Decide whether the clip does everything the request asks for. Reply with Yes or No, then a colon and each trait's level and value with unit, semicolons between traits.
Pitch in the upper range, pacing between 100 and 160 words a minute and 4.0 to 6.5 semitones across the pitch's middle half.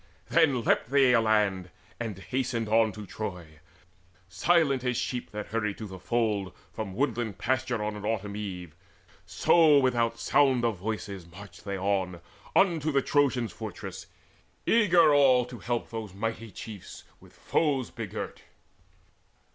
No: low, 115 Hz; average, 140 wpm; average, 4.5 semitones